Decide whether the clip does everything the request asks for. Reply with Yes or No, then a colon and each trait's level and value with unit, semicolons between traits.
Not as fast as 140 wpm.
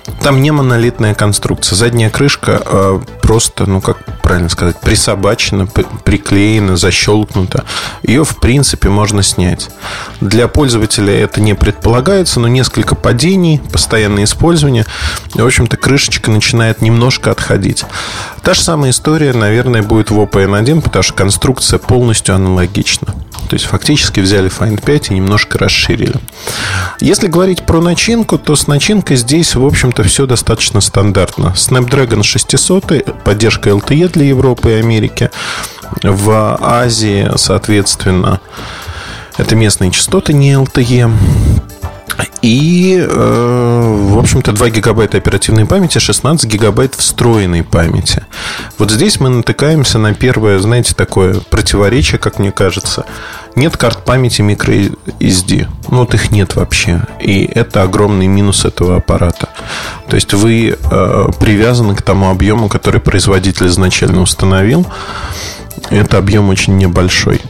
Yes: average, 130 wpm